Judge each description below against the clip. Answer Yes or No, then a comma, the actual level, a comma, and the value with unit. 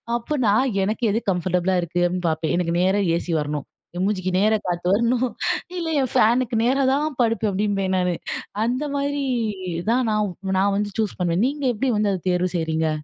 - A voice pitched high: Yes, high, 205 Hz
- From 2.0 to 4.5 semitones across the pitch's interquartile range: No, average, 5.1 semitones